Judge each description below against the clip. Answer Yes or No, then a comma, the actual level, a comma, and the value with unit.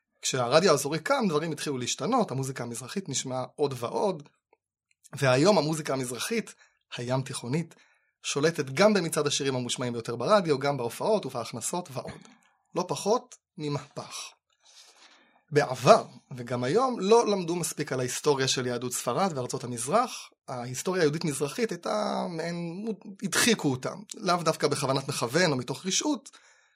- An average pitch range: No, wide, 7.2 semitones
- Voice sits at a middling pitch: Yes, medium, 150 Hz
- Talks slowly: No, average, 125 wpm